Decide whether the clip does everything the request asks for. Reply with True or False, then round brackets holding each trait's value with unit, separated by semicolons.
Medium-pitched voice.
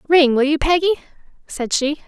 False (300 Hz)